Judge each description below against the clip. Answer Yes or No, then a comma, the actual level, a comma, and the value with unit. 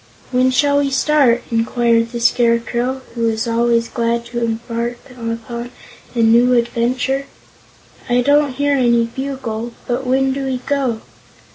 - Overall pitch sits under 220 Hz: No, high, 240 Hz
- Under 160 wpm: Yes, average, 140 wpm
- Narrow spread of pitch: Yes, narrow, 2.2 semitones